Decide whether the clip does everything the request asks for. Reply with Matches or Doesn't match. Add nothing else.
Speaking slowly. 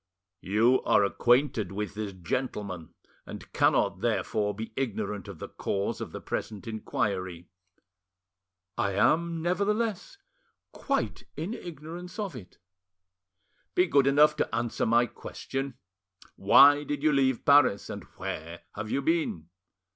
Matches